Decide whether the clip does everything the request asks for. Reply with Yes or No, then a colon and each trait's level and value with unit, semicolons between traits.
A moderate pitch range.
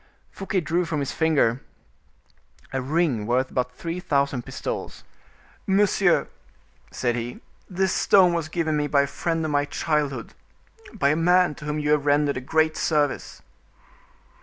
Yes: average, 3.4 semitones